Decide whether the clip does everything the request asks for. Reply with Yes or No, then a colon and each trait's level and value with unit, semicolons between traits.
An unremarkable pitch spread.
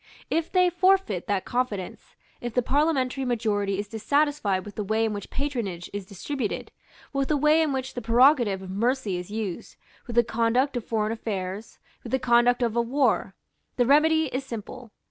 Yes: average, 4.8 semitones